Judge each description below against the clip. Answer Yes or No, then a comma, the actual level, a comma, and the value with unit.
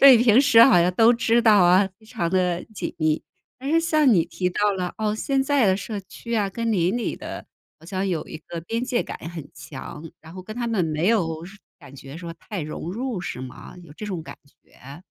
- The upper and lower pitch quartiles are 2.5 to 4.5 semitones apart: No, wide, 5.6 semitones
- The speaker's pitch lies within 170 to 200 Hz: Yes, high, 190 Hz